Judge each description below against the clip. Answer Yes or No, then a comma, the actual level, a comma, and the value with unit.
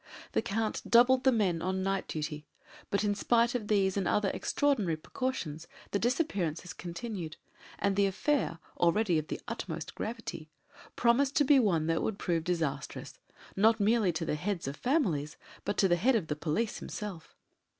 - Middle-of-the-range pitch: No, high, 195 Hz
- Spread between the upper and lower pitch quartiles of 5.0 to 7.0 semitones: Yes, wide, 5.6 semitones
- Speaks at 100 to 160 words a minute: No, average, 170 wpm